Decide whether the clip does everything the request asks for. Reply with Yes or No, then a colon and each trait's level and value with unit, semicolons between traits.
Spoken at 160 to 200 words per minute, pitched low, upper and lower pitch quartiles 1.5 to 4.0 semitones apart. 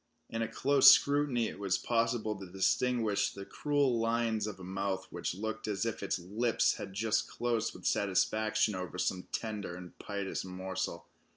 Yes: average, 170 wpm; low, 105 Hz; average, 3.2 semitones